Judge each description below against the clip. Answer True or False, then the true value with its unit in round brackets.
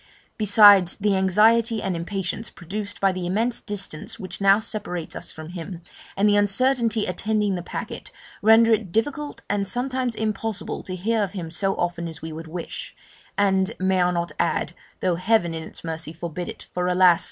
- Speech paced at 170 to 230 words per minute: True (180 wpm)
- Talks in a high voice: True (195 Hz)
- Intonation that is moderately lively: True (3.6 semitones)